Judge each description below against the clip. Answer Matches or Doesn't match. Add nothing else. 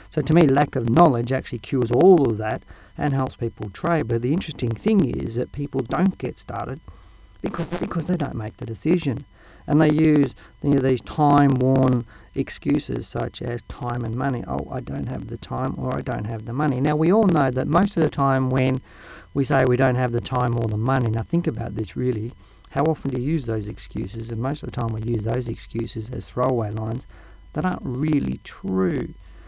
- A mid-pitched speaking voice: Doesn't match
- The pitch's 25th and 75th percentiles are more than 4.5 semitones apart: Doesn't match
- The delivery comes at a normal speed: Doesn't match